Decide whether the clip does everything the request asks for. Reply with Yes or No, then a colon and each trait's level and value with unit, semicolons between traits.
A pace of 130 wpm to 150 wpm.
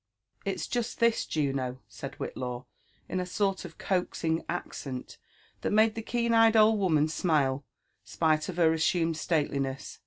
Yes: average, 145 wpm